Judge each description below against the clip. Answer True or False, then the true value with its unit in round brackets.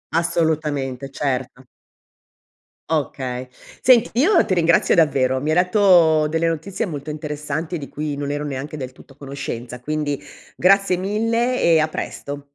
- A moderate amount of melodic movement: True (3.7 semitones)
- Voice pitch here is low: False (155 Hz)